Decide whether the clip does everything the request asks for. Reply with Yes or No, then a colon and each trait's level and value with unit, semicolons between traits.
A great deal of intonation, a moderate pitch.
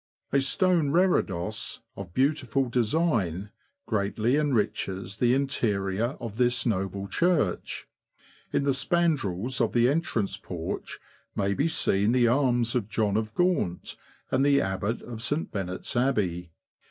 No: wide, 5.7 semitones; low, 120 Hz